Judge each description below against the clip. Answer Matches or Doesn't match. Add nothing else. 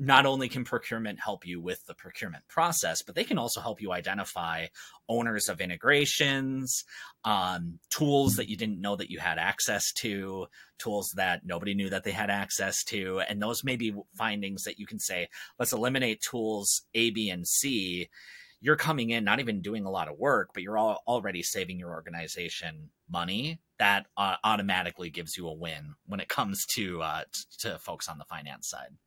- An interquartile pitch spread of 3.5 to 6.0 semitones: Matches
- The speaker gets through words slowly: Doesn't match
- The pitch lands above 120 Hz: Doesn't match